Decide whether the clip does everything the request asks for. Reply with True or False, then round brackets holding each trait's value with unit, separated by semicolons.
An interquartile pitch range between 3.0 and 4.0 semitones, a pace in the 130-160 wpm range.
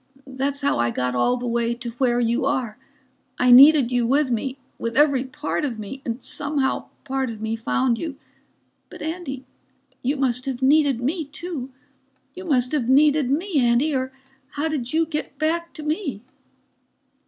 False (3.5 semitones; 175 wpm)